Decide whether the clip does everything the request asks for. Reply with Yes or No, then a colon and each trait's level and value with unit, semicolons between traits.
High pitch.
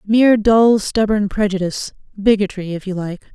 Yes: high, 205 Hz